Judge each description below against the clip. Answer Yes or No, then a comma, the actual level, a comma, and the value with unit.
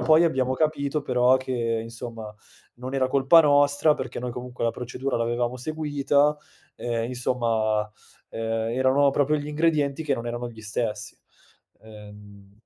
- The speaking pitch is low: Yes, low, 125 Hz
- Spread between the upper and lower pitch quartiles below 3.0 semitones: No, average, 3.7 semitones